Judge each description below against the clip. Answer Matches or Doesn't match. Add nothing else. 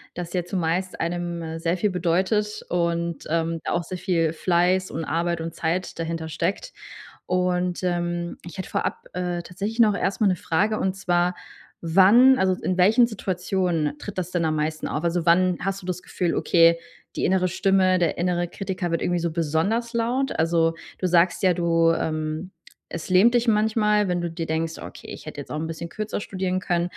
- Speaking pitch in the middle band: Matches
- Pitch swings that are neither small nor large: Doesn't match